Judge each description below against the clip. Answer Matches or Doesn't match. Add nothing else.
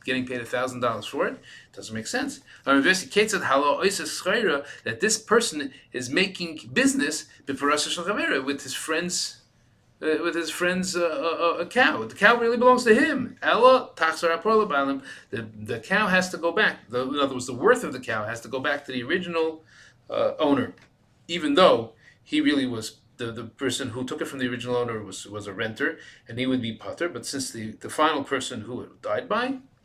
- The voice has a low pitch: Doesn't match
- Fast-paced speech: Doesn't match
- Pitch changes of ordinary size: Doesn't match